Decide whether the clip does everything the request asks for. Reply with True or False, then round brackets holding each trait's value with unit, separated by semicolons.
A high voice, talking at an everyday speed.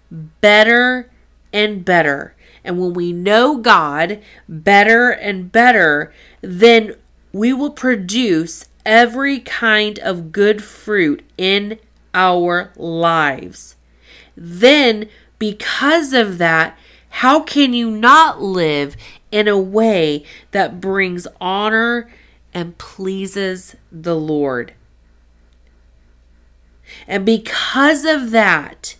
False (200 Hz; 95 wpm)